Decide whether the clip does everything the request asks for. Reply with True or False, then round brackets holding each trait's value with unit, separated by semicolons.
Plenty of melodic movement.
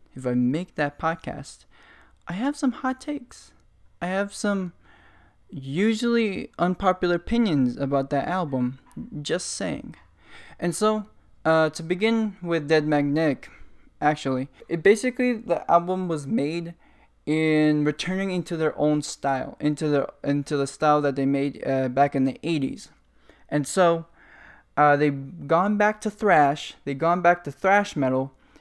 False (4.6 semitones)